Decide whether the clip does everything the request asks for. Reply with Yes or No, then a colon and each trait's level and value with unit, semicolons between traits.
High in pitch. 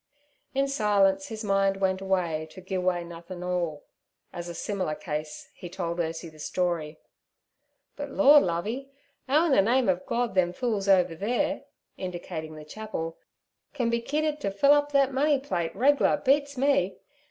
Yes: high, 195 Hz